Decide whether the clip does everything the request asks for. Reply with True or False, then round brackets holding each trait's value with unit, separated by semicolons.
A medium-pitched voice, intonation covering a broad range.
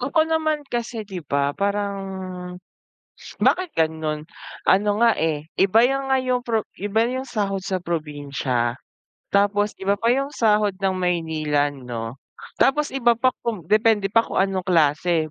False (195 Hz; 6.6 semitones)